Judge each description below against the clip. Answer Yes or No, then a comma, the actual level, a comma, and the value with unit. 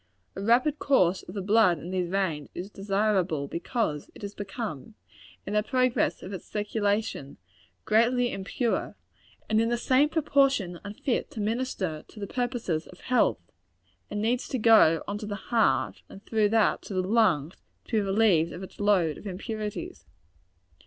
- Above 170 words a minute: No, average, 165 wpm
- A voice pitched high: Yes, high, 205 Hz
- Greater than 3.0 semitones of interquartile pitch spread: Yes, average, 3.7 semitones